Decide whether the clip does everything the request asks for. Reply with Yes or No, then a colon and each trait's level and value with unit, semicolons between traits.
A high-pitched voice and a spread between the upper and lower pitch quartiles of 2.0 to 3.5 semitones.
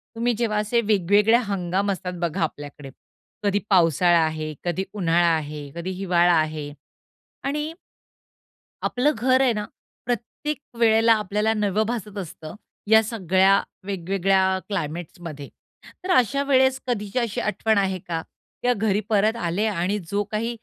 No: high, 200 Hz; average, 4.4 semitones